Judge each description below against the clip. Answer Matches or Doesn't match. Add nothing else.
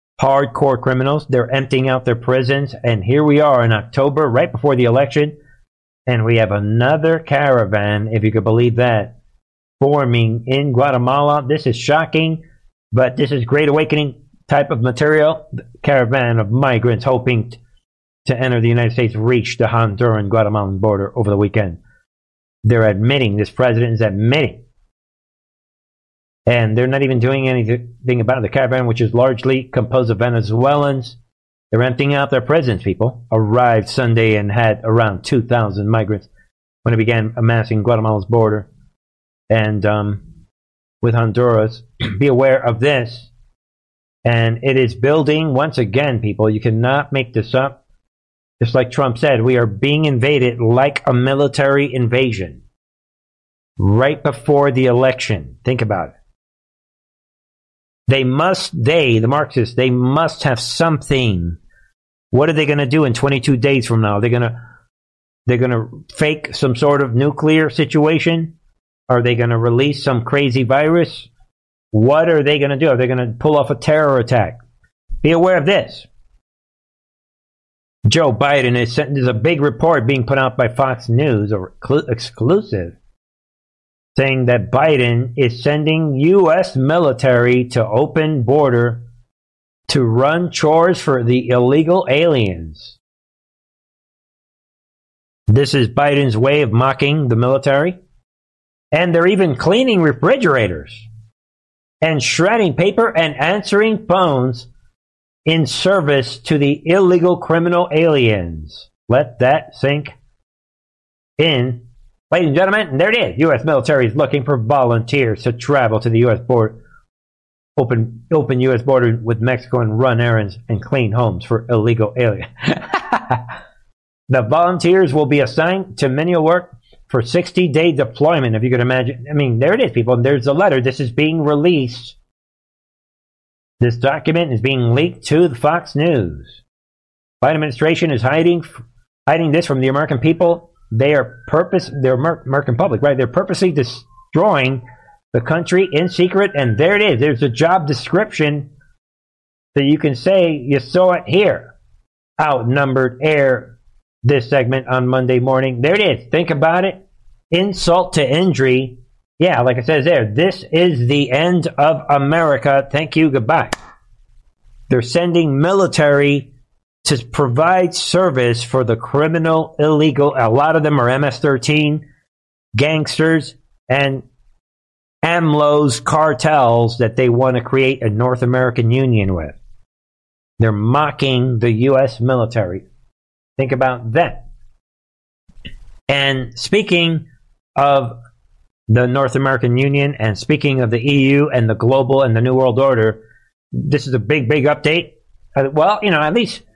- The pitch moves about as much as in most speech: Matches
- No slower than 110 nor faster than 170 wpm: Matches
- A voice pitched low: Matches